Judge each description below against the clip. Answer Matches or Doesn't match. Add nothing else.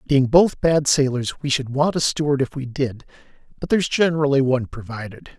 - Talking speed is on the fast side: Doesn't match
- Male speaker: Matches